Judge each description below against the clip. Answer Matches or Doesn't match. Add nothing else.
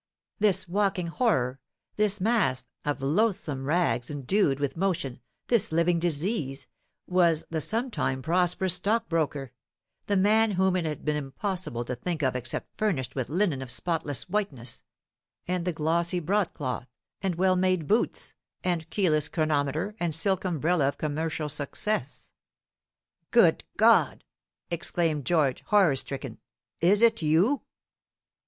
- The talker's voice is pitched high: Doesn't match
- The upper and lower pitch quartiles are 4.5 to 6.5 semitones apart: Matches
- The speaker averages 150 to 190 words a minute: Doesn't match